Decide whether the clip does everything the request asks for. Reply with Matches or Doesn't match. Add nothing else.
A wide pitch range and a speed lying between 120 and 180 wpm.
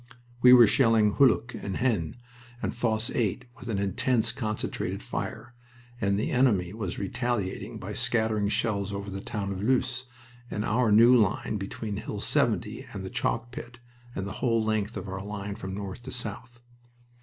Doesn't match